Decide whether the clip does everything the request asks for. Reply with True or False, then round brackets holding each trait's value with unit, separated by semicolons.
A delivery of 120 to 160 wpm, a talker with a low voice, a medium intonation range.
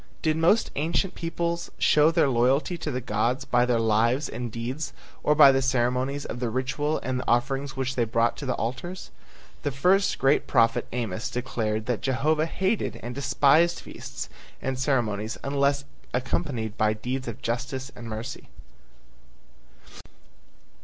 True (155 wpm; 130 Hz; 3.4 semitones)